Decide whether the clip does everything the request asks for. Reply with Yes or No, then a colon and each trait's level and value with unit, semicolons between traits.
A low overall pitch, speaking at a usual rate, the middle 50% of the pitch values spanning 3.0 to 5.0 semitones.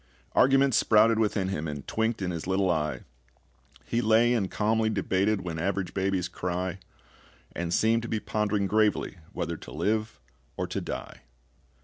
Yes: low, 100 Hz; average, 155 wpm; average, 3.4 semitones